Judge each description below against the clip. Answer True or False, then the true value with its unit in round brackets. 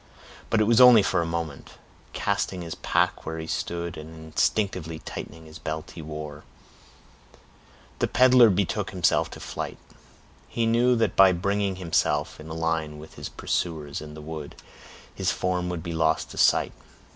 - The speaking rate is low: False (170 wpm)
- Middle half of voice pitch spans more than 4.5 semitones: False (3.9 semitones)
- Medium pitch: False (85 Hz)